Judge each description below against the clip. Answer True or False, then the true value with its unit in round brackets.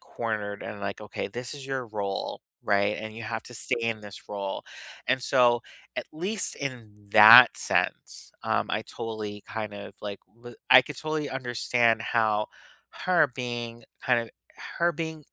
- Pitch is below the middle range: True (115 Hz)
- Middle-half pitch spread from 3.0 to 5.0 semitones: True (3.4 semitones)